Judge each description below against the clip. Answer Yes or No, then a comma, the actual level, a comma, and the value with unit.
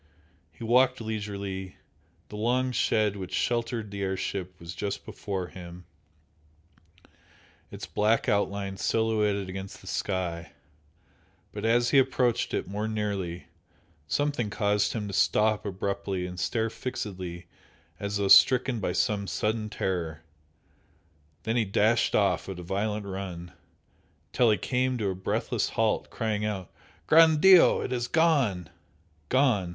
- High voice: No, low, 105 Hz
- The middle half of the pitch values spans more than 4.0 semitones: No, average, 3.4 semitones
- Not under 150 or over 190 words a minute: No, slow, 135 wpm